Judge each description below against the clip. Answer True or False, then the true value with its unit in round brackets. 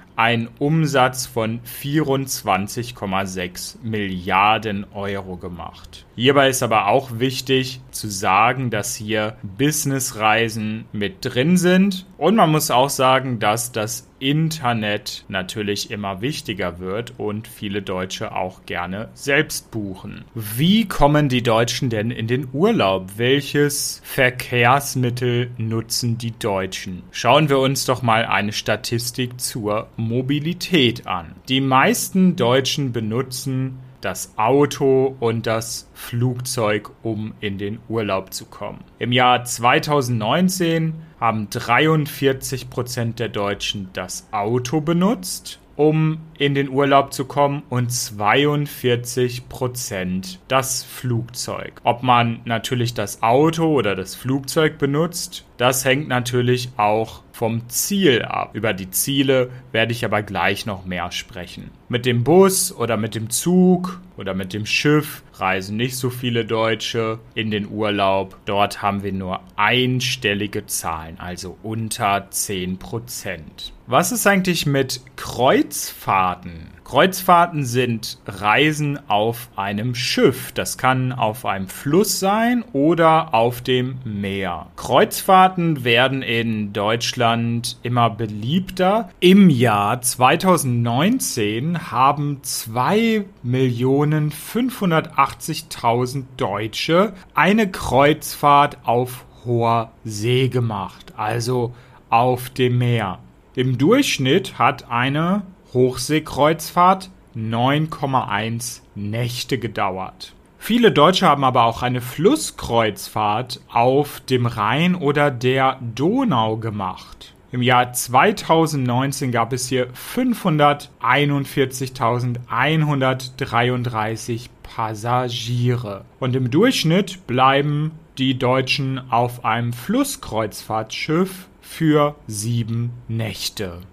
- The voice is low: True (125 Hz)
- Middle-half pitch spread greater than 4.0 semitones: True (4.5 semitones)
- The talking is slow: True (105 wpm)